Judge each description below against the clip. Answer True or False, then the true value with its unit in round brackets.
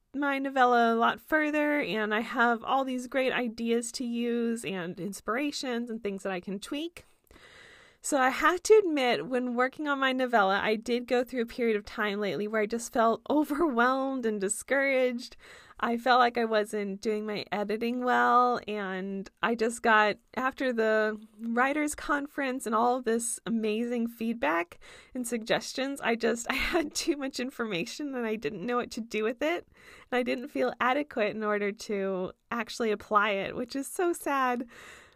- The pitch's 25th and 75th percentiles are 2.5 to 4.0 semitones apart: True (3.4 semitones)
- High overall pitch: True (235 Hz)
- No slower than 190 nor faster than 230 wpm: False (175 wpm)